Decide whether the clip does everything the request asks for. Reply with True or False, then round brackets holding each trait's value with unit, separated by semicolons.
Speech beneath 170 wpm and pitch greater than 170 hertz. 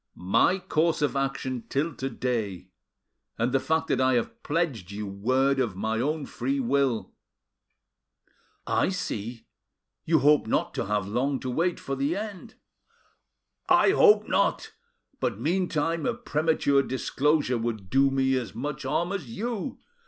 False (150 wpm; 135 Hz)